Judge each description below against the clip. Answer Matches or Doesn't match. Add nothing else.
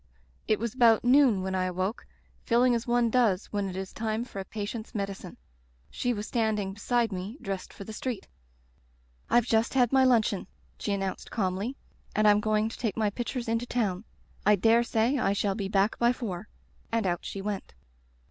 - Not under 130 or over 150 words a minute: Doesn't match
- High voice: Matches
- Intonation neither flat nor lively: Matches